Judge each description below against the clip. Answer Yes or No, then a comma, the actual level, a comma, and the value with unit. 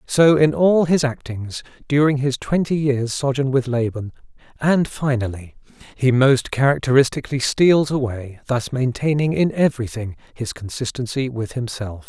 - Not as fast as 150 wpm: Yes, average, 140 wpm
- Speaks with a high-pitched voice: No, low, 130 Hz